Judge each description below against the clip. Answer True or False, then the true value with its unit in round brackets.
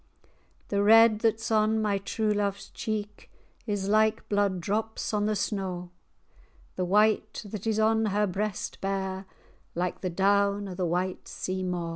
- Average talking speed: True (165 wpm)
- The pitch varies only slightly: True (2.2 semitones)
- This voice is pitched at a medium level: False (205 Hz)